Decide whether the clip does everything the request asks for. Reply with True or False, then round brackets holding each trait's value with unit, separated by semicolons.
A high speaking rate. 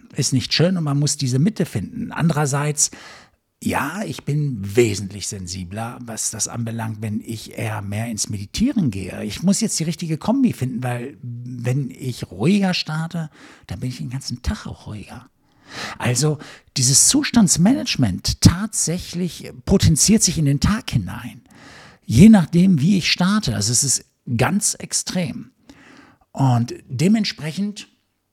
False (140 wpm)